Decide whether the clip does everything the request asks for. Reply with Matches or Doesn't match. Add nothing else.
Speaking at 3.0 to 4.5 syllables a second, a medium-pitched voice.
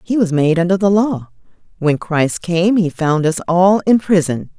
Matches